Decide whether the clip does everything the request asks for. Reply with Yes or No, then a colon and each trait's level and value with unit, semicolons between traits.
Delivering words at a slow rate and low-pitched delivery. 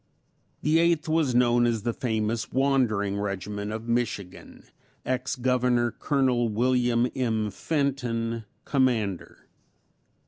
Yes: slow, 105 wpm; low, 120 Hz